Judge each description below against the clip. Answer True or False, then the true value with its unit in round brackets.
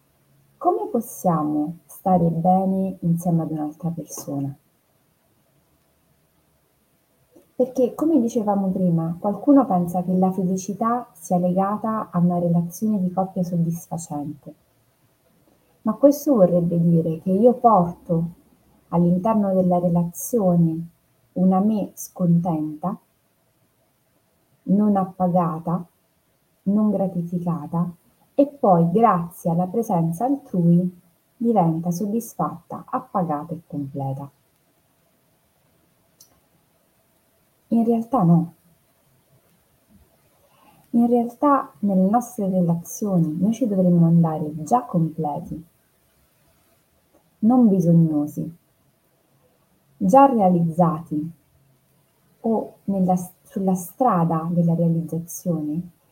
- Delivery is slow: True (80 wpm)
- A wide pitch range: False (3.6 semitones)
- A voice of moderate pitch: True (180 Hz)